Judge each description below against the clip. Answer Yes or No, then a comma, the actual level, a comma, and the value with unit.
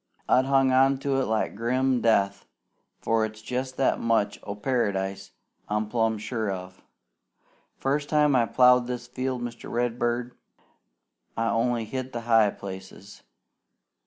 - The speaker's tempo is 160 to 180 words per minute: No, average, 140 wpm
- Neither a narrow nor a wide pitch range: Yes, average, 3.2 semitones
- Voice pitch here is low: Yes, low, 120 Hz